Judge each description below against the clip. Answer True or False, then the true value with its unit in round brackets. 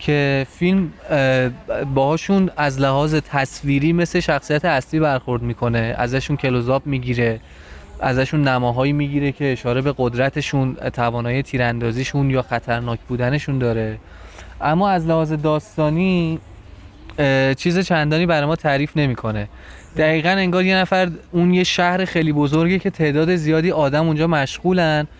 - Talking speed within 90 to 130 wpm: True (125 wpm)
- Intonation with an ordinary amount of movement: True (4.3 semitones)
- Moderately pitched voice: True (145 Hz)